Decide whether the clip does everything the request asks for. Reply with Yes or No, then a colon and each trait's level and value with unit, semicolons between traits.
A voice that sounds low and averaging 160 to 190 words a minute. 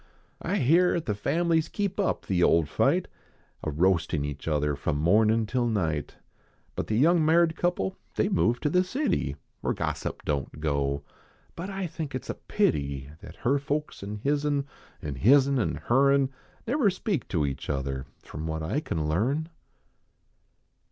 Yes: low, 120 Hz; average, 180 wpm